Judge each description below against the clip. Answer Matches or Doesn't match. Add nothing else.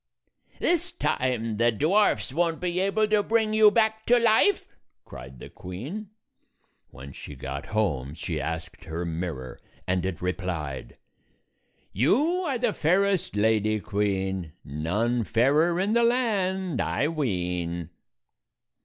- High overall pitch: Doesn't match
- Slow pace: Matches